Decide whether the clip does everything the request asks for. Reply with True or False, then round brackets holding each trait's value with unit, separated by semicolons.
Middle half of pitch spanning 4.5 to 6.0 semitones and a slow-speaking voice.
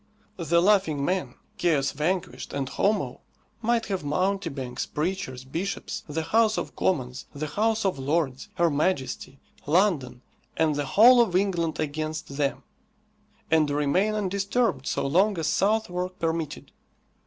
True (5.3 semitones; 130 wpm)